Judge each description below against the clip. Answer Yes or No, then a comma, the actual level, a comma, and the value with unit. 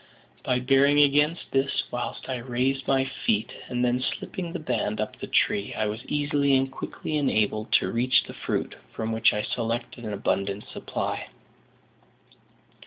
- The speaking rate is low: No, average, 160 wpm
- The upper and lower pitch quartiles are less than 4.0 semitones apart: Yes, average, 3.6 semitones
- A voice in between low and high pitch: No, low, 125 Hz